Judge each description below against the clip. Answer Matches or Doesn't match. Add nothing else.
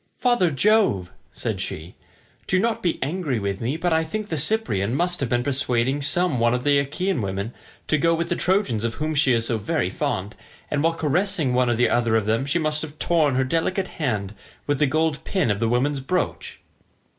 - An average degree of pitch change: Doesn't match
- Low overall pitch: Doesn't match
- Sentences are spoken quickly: Matches